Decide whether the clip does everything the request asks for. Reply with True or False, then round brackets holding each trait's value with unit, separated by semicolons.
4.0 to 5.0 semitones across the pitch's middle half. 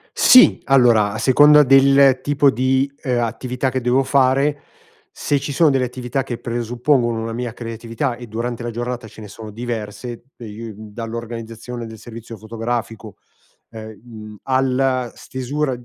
False (2.6 semitones)